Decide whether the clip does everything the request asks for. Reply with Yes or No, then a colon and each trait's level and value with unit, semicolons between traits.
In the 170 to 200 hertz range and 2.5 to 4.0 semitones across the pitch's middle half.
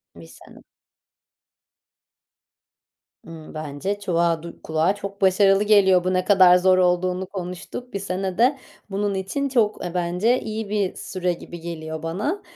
Yes: medium, 185 Hz; average, 2.9 semitones